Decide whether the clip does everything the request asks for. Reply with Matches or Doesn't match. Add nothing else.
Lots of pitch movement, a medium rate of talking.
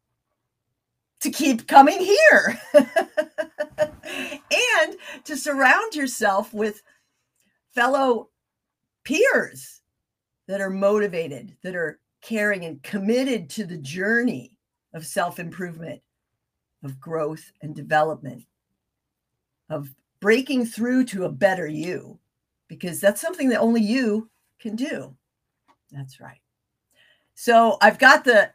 Doesn't match